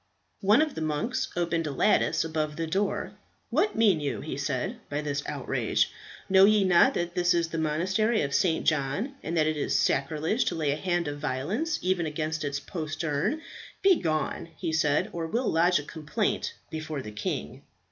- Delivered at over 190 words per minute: No, average, 185 wpm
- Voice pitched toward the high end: No, medium, 160 Hz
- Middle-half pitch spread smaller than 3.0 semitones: No, average, 4.0 semitones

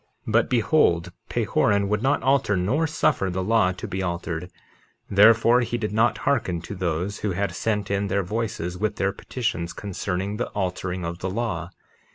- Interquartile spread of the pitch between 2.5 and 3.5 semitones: No, average, 3.9 semitones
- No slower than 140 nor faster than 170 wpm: No, average, 180 wpm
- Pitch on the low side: Yes, low, 100 Hz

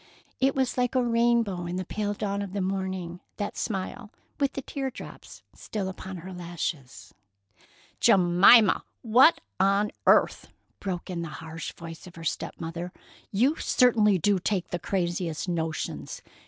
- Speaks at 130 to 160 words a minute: Yes, average, 155 wpm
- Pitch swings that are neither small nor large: Yes, average, 4.5 semitones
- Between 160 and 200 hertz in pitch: Yes, high, 190 Hz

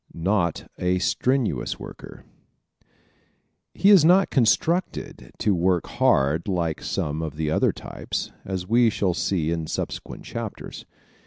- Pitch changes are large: Yes, wide, 6.6 semitones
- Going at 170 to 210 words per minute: No, slow, 135 wpm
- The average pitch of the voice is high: No, very low, 90 Hz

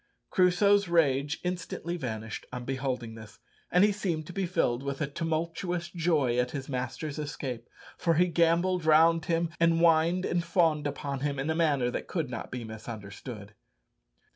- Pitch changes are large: No, average, 4.8 semitones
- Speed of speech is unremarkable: Yes, average, 165 wpm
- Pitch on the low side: No, medium, 155 Hz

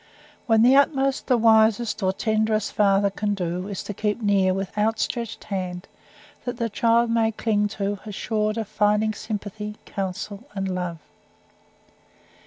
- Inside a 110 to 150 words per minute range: Yes, average, 145 wpm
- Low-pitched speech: No, high, 210 Hz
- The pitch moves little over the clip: Yes, narrow, 2.2 semitones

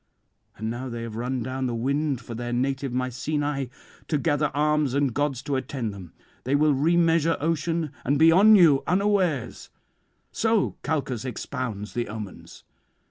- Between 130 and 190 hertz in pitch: Yes, medium, 140 Hz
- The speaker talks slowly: No, average, 155 wpm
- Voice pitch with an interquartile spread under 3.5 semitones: No, average, 4.1 semitones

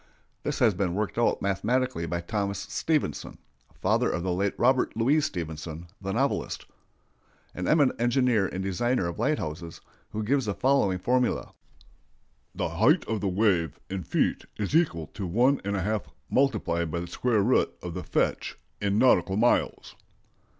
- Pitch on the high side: No, low, 100 Hz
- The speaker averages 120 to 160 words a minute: Yes, average, 150 wpm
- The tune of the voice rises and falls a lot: Yes, wide, 5.7 semitones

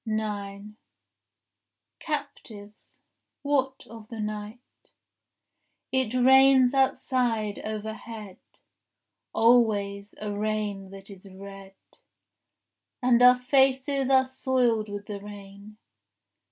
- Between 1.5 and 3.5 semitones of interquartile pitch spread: No, average, 4.0 semitones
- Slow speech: Yes, slow, 85 wpm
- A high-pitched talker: Yes, high, 215 Hz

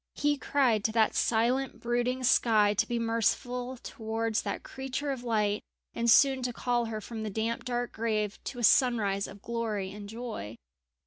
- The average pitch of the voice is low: No, high, 230 Hz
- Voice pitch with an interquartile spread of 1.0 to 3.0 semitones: Yes, narrow, 2.4 semitones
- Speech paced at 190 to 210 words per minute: No, average, 175 wpm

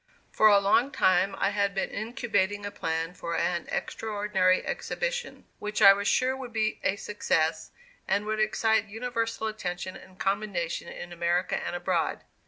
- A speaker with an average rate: Yes, average, 160 wpm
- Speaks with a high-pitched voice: Yes, high, 200 Hz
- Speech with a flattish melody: No, average, 3.2 semitones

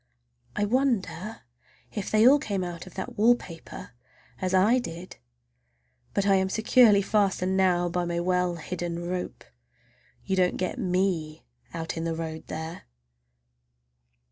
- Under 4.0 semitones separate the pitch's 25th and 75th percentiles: Yes, average, 2.9 semitones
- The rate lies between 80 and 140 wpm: Yes, slow, 135 wpm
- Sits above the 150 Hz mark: Yes, medium, 185 Hz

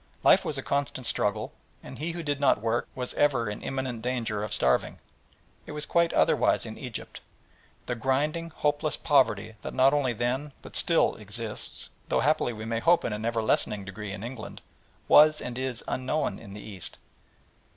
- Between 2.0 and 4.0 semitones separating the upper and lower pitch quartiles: No, average, 4.8 semitones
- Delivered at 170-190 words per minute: Yes, average, 180 wpm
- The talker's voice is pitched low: Yes, low, 125 Hz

